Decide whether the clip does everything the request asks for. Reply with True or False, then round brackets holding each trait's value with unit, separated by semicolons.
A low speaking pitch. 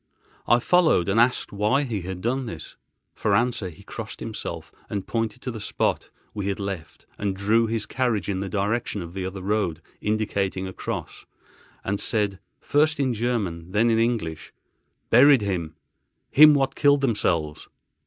True (105 Hz)